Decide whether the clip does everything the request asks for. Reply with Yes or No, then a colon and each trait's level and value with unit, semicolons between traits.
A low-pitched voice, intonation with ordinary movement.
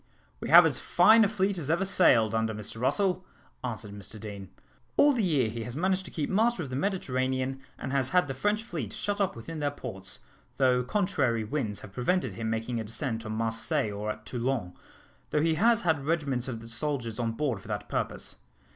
No: low, 130 Hz; wide, 7.5 semitones